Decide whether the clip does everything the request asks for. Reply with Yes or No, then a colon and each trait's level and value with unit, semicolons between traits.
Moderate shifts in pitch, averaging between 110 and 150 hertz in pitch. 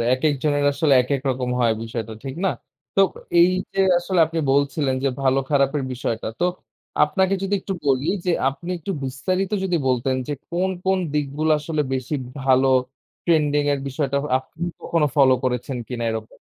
Yes: average, 4.0 semitones; medium, 140 Hz